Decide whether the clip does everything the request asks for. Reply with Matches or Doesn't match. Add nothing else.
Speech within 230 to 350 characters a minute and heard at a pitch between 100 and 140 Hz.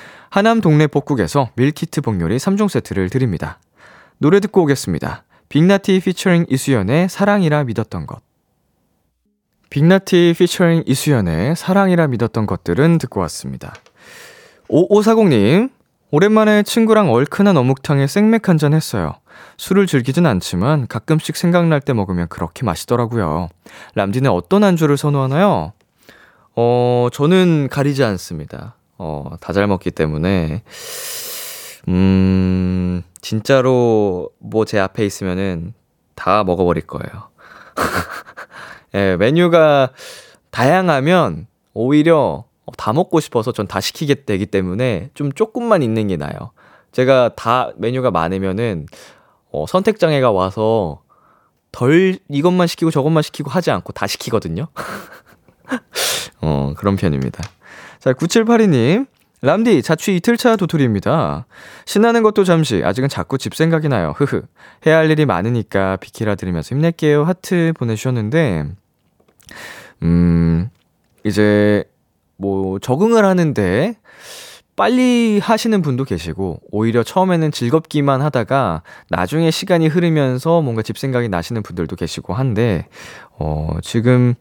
Matches